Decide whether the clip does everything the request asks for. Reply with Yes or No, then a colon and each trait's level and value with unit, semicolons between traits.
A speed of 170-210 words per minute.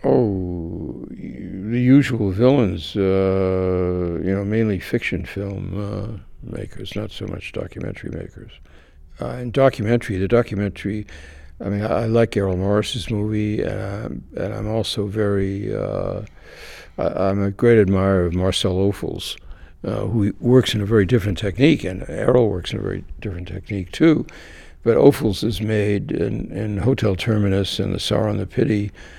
No: average, 155 wpm